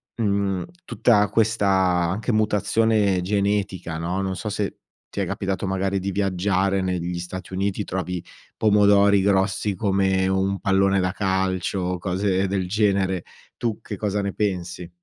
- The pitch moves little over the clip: Yes, narrow, 1.6 semitones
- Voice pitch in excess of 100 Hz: No, very low, 95 Hz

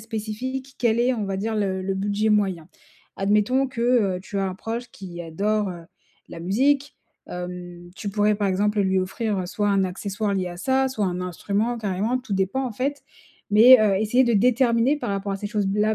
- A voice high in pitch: Yes, high, 210 Hz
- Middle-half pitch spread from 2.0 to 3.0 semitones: No, average, 3.6 semitones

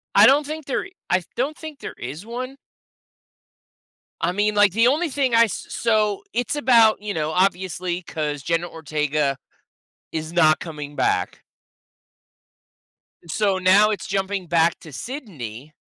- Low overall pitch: No, high, 190 Hz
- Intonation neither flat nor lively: No, wide, 6.5 semitones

